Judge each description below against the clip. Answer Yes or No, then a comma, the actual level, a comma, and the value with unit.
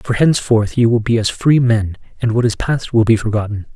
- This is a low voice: Yes, low, 115 Hz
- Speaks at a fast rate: Yes, fast, 240 wpm